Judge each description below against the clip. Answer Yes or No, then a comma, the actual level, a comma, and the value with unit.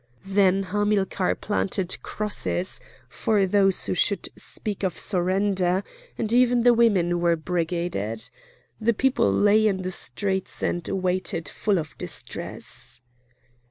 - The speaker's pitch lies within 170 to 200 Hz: Yes, high, 190 Hz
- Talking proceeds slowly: Yes, slow, 125 wpm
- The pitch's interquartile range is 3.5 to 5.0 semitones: No, average, 2.8 semitones